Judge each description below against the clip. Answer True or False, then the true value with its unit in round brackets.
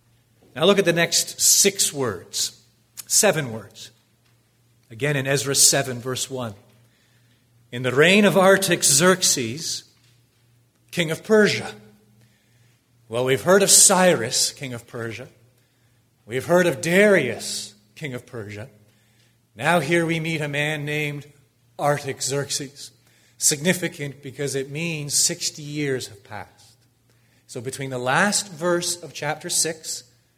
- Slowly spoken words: True (120 wpm)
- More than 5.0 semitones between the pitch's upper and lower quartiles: True (5.4 semitones)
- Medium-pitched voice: False (130 Hz)